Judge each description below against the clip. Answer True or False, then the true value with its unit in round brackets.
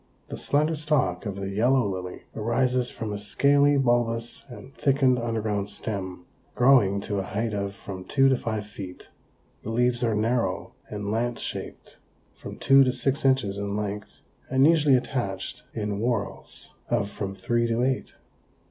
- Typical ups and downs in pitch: True (4.2 semitones)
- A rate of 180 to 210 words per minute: False (160 wpm)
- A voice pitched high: False (115 Hz)